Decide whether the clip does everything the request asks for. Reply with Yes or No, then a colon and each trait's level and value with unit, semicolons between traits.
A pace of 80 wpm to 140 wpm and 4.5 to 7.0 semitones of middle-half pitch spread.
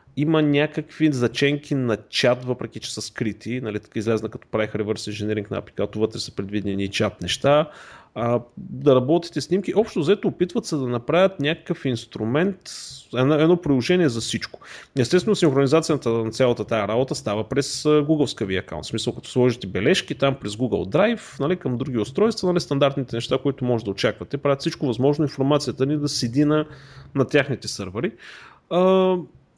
No: fast, 165 wpm; average, 5.1 semitones